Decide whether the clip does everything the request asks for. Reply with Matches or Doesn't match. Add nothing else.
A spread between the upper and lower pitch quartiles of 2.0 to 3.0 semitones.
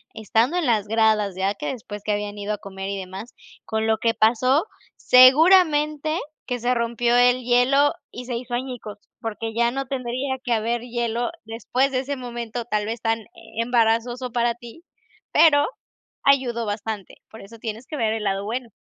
Matches